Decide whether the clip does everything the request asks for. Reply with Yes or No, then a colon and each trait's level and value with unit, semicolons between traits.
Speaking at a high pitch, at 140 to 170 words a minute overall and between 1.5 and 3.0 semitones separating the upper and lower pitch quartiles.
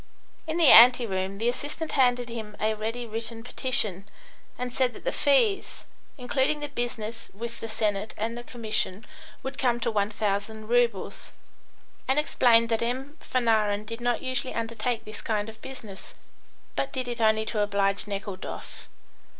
Yes: high, 230 Hz; average, 160 wpm; average, 2.7 semitones